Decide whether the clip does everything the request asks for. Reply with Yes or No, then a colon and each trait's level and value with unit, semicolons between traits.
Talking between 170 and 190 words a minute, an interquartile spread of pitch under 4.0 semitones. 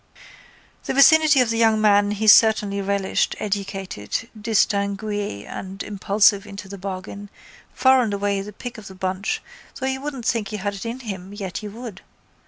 Yes: average, 175 wpm; narrow, 2.4 semitones